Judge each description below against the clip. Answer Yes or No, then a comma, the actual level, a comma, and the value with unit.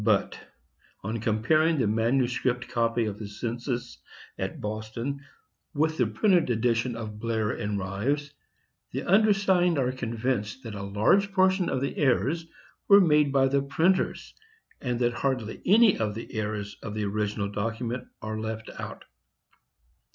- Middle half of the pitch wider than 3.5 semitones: Yes, average, 4.8 semitones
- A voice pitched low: Yes, low, 120 Hz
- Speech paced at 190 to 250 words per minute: No, average, 145 wpm